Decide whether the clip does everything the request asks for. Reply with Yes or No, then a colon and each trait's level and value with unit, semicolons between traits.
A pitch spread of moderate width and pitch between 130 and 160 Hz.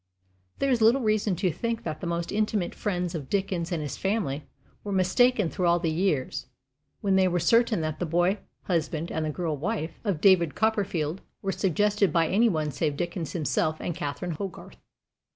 No: average, 4.1 semitones; medium, 180 Hz